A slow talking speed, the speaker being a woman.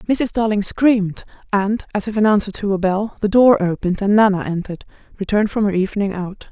No: fast, 205 wpm; female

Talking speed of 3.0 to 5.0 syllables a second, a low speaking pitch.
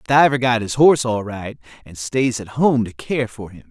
Yes: 4.9 syllables/s; low, 115 Hz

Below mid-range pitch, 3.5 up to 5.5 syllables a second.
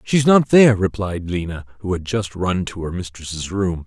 Yes: low, 100 Hz; 5.0 syllables/s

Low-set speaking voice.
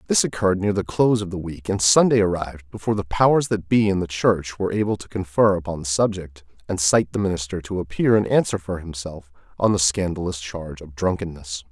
Yes: very low, 90 Hz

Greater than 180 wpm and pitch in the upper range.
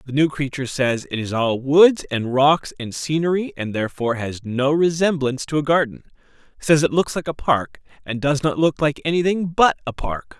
No: average, 200 wpm; medium, 145 Hz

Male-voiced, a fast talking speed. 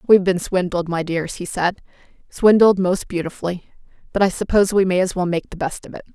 No: female; fast, 215 wpm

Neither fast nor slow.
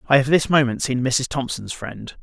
No: fast, 215 wpm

